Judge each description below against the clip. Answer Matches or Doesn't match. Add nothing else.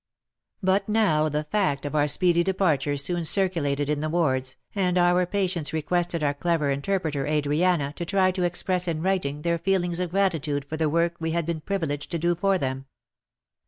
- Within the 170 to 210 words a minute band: Matches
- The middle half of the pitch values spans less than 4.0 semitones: Matches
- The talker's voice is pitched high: Doesn't match